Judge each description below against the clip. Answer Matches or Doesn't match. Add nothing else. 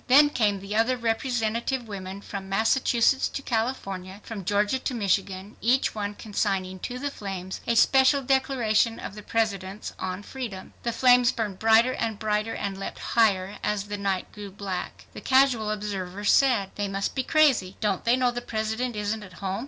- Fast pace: Doesn't match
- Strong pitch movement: Doesn't match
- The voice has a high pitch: Matches